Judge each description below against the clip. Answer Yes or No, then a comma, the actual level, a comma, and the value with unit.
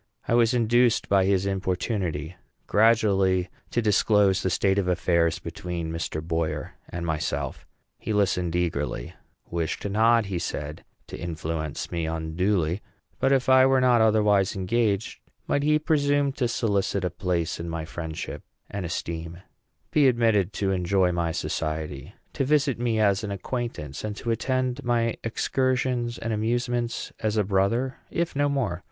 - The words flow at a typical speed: Yes, average, 150 wpm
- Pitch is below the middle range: Yes, low, 100 Hz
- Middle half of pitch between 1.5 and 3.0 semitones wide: No, wide, 5.6 semitones